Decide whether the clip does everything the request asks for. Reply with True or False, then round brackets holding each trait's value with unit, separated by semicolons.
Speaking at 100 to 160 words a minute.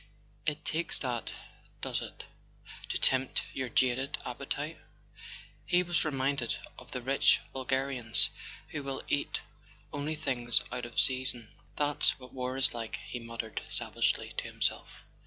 True (140 wpm)